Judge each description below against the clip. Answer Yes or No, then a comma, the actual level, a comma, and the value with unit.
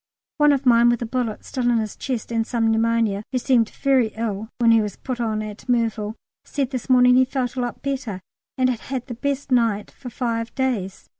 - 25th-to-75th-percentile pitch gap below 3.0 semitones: Yes, narrow, 2.4 semitones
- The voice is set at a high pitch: Yes, high, 240 Hz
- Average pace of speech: No, fast, 220 wpm